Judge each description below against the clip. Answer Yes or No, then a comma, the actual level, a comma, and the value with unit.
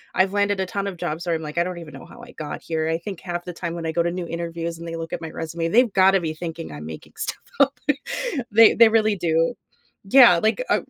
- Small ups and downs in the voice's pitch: No, average, 3.3 semitones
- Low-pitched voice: No, medium, 170 Hz